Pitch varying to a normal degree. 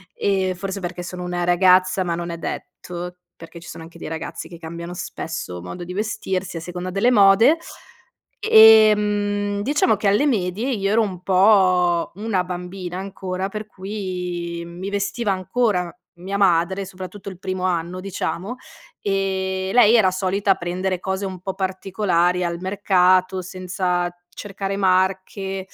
No: narrow, 1.9 semitones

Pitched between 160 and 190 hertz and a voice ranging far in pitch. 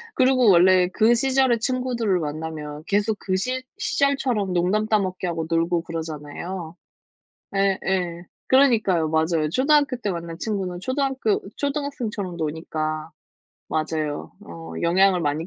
Yes: medium, 185 Hz; wide, 6.5 semitones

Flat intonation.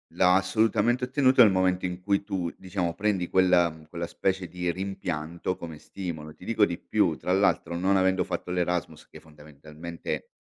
Yes: narrow, 2.3 semitones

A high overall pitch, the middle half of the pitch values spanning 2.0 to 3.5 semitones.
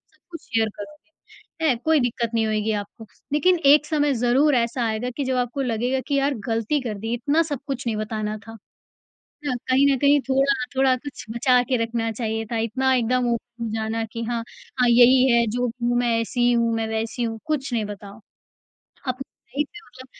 Yes: high, 245 Hz; average, 3.0 semitones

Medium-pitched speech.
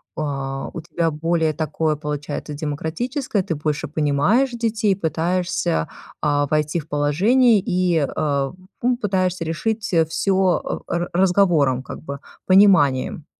Yes: medium, 160 Hz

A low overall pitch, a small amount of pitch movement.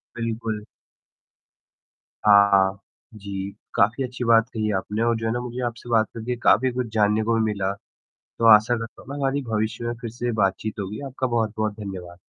Yes: low, 115 Hz; narrow, 2.3 semitones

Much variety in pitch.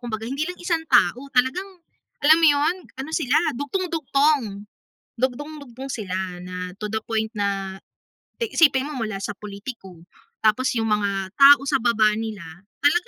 Yes: wide, 5.8 semitones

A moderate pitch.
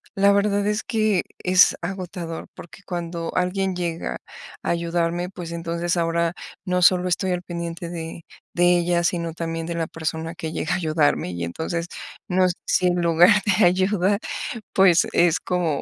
Yes: medium, 175 Hz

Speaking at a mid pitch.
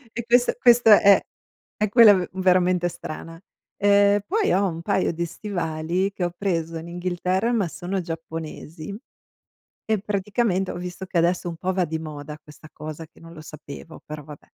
Yes: medium, 180 Hz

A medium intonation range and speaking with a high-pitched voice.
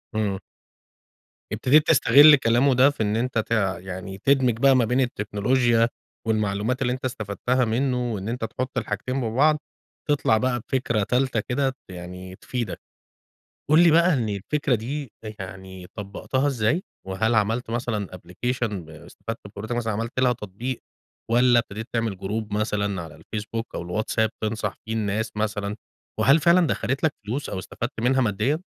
No: average, 3.8 semitones; low, 115 Hz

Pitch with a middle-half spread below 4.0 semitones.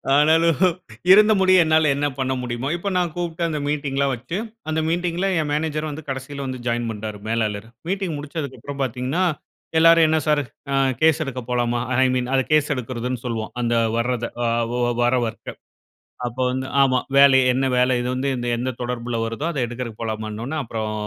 No: average, 4.6 semitones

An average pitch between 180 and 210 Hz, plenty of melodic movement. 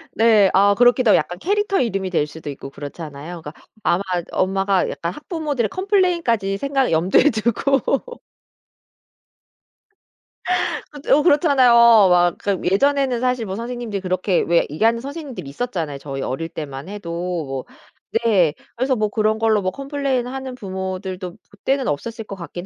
Yes: high, 205 Hz; wide, 6.6 semitones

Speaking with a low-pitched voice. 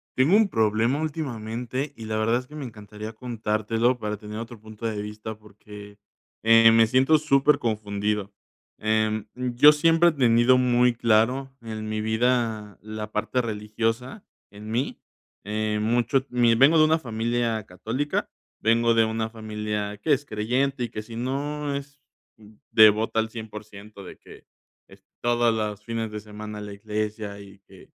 Yes: low, 110 Hz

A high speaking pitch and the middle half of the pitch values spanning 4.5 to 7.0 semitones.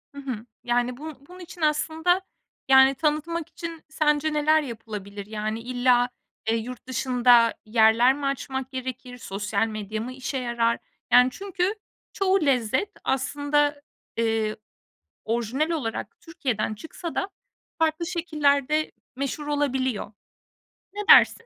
Yes: very high, 265 Hz; average, 4.9 semitones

